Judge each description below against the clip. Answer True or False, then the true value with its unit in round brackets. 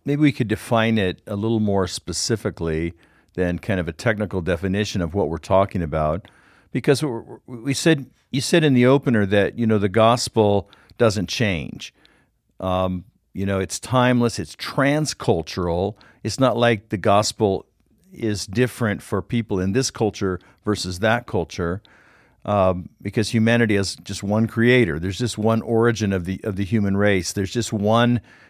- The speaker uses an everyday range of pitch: True (3.7 semitones)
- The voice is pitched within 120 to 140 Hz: False (105 Hz)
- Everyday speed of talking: True (160 wpm)